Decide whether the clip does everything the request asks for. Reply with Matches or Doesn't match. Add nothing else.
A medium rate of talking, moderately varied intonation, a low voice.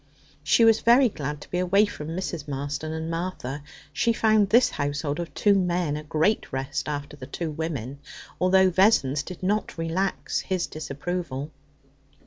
Doesn't match